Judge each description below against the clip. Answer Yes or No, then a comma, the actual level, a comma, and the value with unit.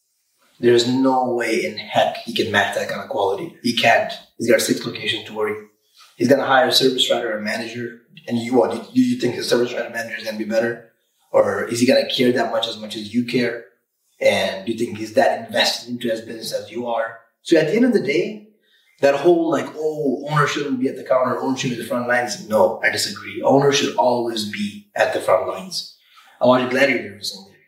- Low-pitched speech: Yes, low, 120 Hz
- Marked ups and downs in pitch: No, average, 3.5 semitones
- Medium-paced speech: No, fast, 240 wpm